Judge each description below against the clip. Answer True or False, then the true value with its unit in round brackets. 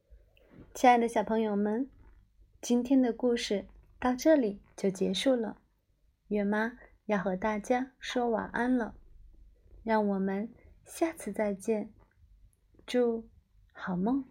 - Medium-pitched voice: False (220 Hz)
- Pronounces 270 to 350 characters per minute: False (165 characters per minute)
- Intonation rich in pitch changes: False (3.9 semitones)